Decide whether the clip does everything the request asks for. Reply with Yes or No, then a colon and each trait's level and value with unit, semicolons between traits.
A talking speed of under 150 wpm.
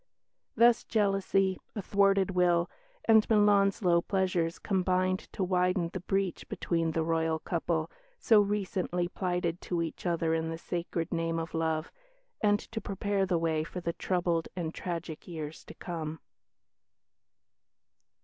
Yes: average, 140 wpm